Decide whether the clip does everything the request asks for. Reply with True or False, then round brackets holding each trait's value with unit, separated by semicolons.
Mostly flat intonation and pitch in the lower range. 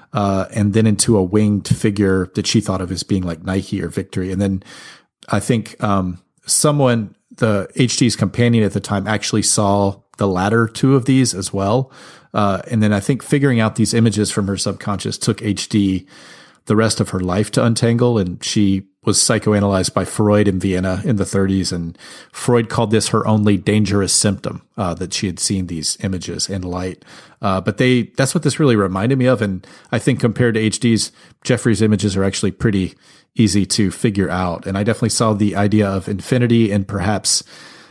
False (3.0 semitones; 105 Hz)